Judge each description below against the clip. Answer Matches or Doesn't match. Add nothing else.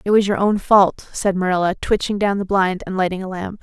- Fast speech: Matches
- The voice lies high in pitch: Matches